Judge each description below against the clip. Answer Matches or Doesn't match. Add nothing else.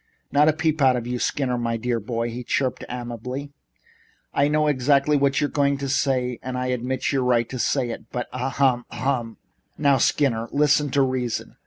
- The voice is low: Matches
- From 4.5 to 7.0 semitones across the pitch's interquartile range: Doesn't match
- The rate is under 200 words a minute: Doesn't match